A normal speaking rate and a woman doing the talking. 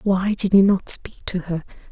No: fast, 220 wpm; female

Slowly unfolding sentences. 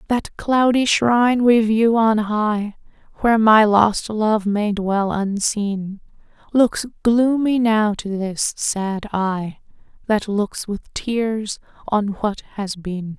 Yes: slow, 130 wpm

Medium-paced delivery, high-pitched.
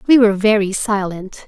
Yes: average, 165 wpm; high, 205 Hz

